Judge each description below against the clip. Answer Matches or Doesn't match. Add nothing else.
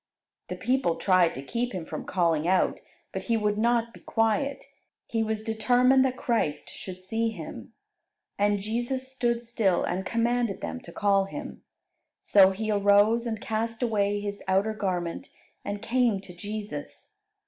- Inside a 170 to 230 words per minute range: Doesn't match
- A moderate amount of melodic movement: Matches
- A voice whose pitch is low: Doesn't match